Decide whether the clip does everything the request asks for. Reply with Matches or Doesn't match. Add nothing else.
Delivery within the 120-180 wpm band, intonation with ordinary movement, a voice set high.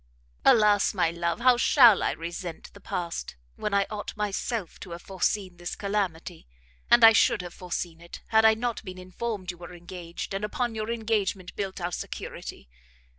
Matches